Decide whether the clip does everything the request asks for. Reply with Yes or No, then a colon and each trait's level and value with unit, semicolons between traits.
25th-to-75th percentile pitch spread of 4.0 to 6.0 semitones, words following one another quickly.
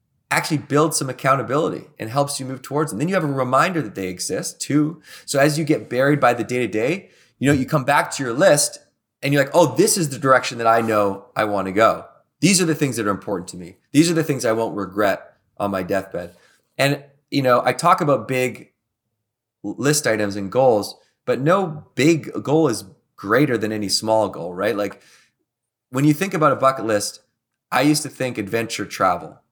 Yes: average, 5.3 semitones; fast, 220 wpm